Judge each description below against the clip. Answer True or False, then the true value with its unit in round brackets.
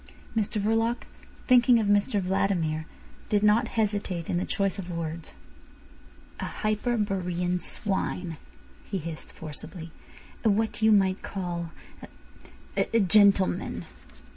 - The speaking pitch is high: True (195 Hz)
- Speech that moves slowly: True (115 wpm)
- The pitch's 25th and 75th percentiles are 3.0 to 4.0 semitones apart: True (3.3 semitones)